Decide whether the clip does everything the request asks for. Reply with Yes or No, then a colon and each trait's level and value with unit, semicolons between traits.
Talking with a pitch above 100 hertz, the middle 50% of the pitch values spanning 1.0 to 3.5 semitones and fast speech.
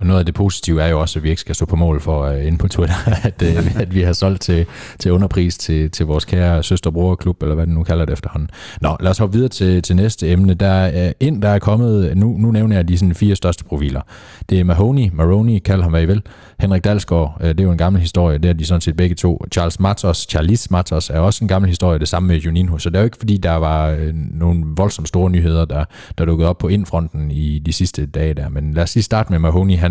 No: very low, 90 Hz; average, 2.9 semitones; fast, 270 wpm